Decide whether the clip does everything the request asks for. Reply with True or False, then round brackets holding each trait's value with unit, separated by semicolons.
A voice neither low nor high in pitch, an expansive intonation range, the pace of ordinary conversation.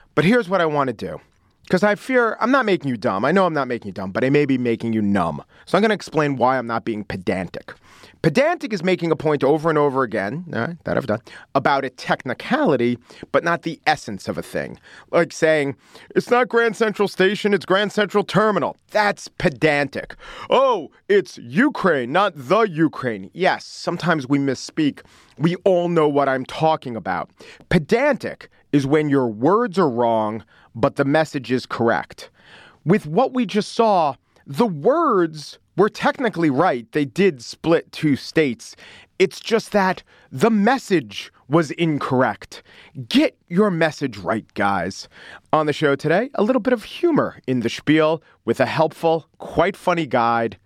True (160 Hz; 7.7 semitones; 180 wpm)